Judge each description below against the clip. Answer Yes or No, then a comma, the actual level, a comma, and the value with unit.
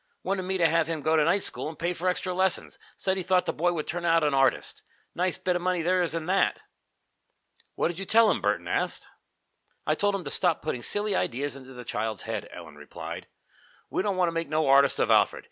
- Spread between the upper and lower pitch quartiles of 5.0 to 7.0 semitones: No, average, 3.8 semitones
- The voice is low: No, medium, 170 Hz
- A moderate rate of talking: No, fast, 240 wpm